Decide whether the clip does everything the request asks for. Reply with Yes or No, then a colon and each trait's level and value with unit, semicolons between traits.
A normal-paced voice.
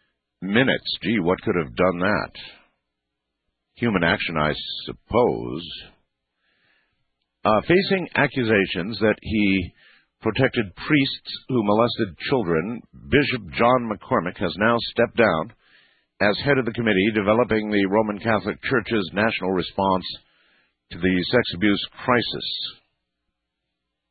No: slow, 110 wpm